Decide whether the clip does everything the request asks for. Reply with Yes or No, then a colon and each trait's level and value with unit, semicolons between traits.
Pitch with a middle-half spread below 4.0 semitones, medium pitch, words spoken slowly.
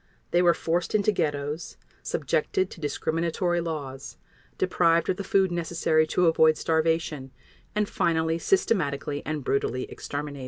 Yes: average, 2.9 semitones; medium, 165 Hz; slow, 130 wpm